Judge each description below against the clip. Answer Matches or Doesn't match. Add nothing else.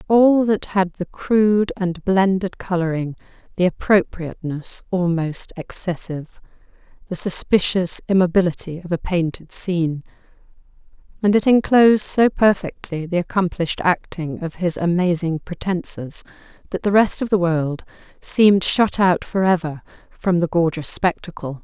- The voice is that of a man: Doesn't match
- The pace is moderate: Doesn't match